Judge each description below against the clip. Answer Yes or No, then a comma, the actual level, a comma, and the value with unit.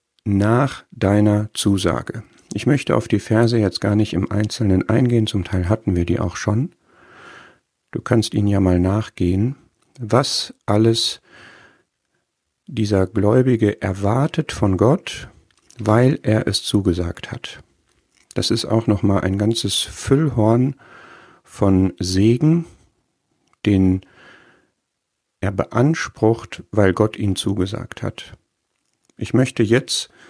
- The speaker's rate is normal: No, slow, 120 wpm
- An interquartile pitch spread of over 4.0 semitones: No, average, 3.2 semitones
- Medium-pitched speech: No, low, 110 Hz